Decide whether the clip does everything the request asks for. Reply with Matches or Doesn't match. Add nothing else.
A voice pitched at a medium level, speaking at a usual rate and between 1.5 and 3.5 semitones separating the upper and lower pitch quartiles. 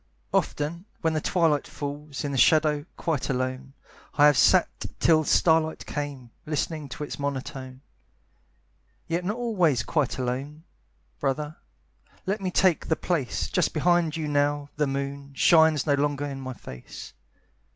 Matches